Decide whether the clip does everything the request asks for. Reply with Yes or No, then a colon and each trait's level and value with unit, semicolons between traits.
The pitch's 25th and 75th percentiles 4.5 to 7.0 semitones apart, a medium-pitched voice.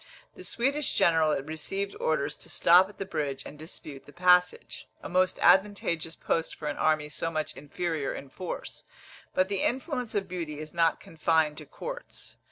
No: average, 3.8 semitones; medium, 170 Hz